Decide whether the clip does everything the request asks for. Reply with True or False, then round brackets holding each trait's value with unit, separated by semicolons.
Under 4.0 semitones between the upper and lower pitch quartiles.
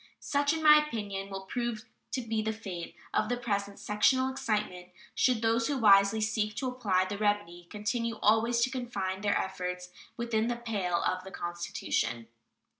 True (3.6 semitones)